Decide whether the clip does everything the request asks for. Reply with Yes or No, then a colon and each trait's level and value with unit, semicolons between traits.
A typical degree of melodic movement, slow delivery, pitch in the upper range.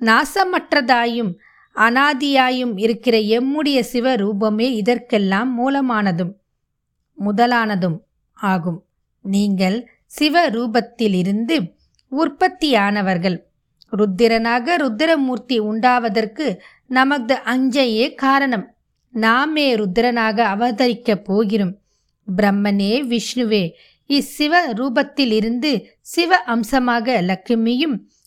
Yes: average, 3.7 semitones; slow, 60 wpm; high, 235 Hz